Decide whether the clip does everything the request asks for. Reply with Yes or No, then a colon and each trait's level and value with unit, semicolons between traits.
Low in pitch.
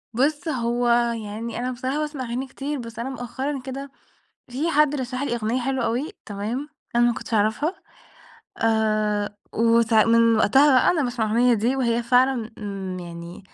No: high, 240 Hz